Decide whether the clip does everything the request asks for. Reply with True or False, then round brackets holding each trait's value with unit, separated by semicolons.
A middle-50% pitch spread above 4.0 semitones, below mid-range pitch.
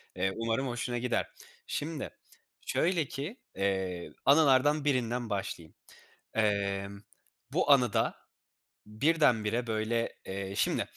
True (5.4 semitones; 115 Hz)